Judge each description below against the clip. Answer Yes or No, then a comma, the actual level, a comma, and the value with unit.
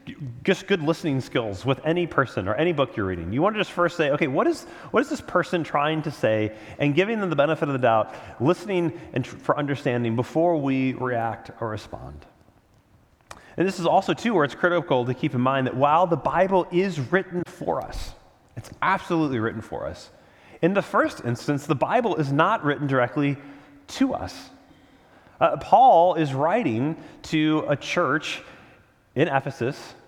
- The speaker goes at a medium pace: Yes, average, 185 wpm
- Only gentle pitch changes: No, wide, 5.4 semitones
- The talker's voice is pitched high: No, medium, 145 Hz